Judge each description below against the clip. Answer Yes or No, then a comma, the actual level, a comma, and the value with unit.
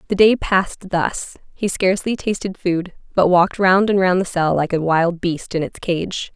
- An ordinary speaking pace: No, fast, 210 wpm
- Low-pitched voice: No, medium, 185 Hz